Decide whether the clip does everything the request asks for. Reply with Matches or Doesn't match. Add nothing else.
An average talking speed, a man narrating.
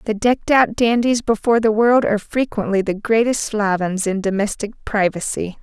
Doesn't match